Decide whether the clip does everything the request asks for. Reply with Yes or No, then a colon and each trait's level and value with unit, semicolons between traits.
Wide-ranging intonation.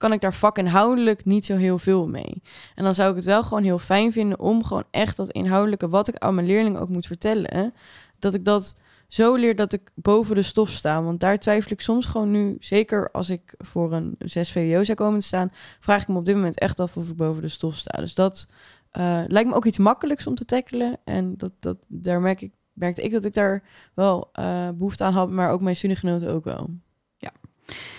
No: average, 2.9 semitones